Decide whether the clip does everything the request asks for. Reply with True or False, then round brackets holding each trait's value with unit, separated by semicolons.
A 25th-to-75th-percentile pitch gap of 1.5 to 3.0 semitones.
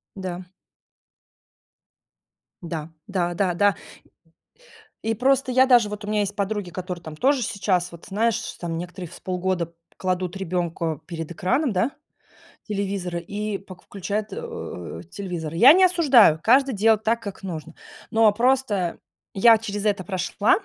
False (3.9 semitones)